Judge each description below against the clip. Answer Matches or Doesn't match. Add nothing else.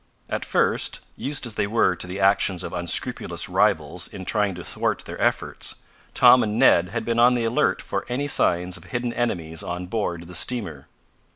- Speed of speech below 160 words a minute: Doesn't match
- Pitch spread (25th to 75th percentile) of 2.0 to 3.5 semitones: Doesn't match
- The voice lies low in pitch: Matches